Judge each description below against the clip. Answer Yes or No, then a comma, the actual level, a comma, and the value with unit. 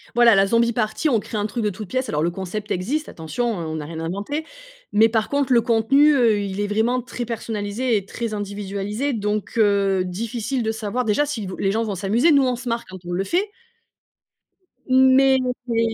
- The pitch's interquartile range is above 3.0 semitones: Yes, average, 3.6 semitones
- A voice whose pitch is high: Yes, high, 220 Hz